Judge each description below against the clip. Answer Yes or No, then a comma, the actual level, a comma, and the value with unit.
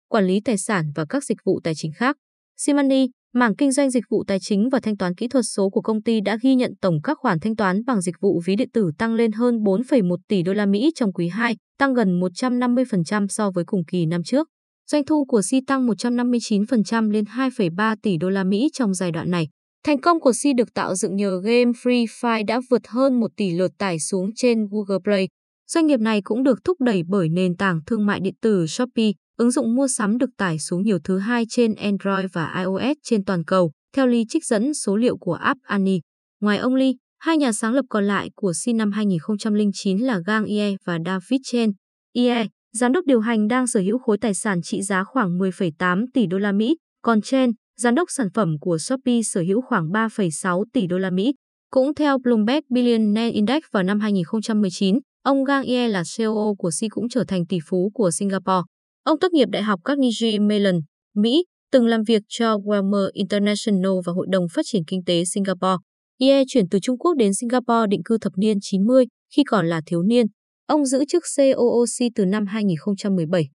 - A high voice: Yes, high, 215 Hz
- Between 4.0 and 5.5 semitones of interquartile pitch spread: Yes, average, 4.3 semitones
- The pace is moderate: Yes, average, 215 wpm